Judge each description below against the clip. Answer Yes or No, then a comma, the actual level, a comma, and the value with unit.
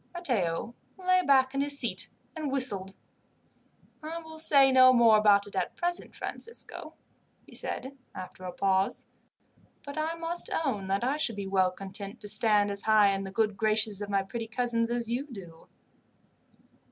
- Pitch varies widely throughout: Yes, wide, 5.8 semitones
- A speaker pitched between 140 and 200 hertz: No, high, 225 Hz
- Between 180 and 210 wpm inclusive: No, average, 170 wpm